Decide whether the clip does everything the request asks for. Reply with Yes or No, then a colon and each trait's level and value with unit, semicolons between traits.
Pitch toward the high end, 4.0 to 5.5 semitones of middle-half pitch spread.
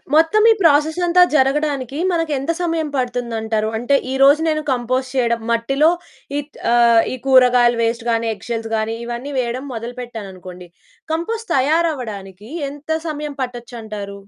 Yes: very high, 250 Hz; average, 4.5 semitones